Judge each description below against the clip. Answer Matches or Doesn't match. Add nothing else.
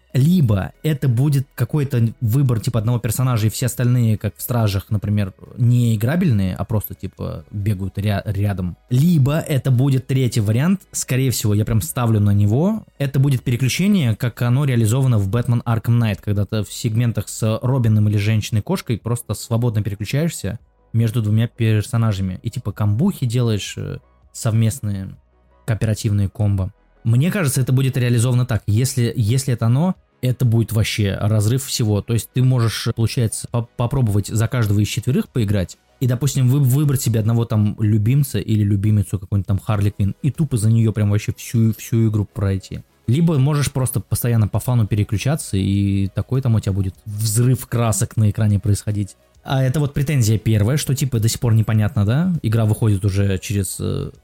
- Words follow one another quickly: Matches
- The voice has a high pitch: Doesn't match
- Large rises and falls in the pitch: Doesn't match